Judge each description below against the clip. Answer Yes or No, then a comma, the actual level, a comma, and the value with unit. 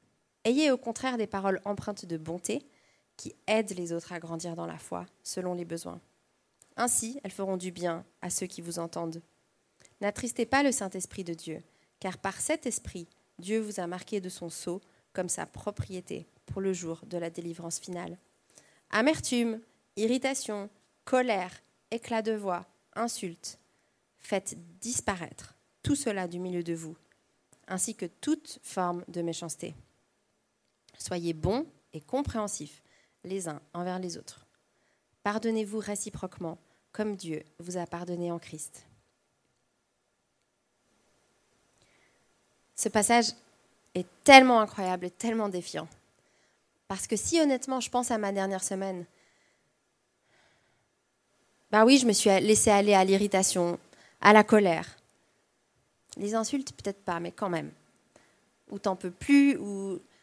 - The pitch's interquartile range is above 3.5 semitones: Yes, average, 4.2 semitones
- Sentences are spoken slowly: Yes, slow, 140 wpm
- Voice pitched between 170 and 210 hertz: Yes, high, 190 Hz